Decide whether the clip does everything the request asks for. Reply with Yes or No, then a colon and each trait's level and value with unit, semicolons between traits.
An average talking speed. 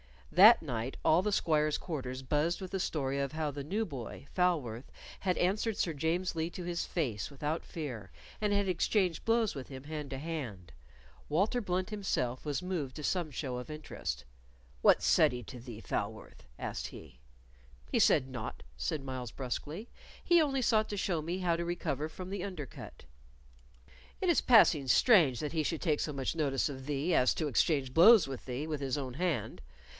Yes: average, 190 wpm